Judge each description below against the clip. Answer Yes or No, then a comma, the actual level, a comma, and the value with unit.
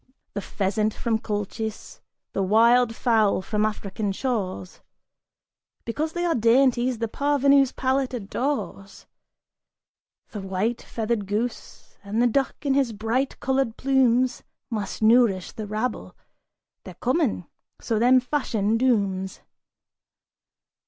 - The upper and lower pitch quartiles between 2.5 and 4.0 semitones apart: Yes, average, 3.5 semitones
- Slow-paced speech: Yes, slow, 115 wpm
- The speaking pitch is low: No, high, 230 Hz